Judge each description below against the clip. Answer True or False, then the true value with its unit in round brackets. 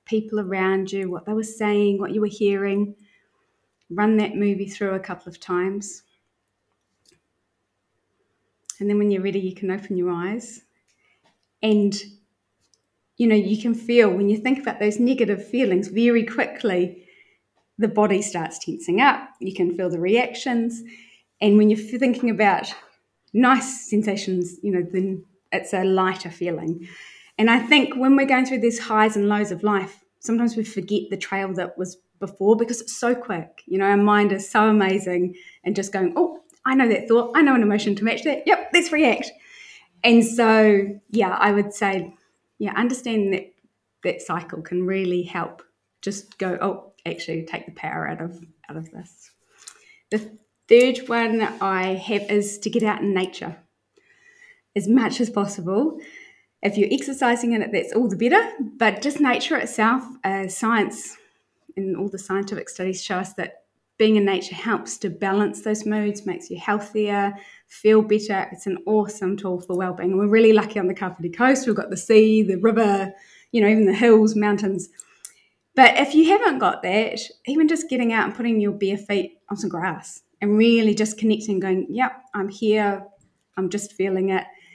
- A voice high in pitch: True (205 Hz)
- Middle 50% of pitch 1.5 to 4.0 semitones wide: True (3.3 semitones)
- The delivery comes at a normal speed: True (180 wpm)